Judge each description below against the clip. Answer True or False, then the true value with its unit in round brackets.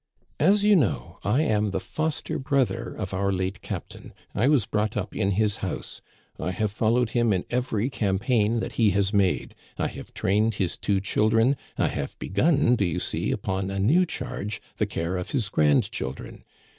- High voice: False (105 Hz)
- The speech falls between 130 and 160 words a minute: False (185 wpm)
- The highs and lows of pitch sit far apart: False (4.1 semitones)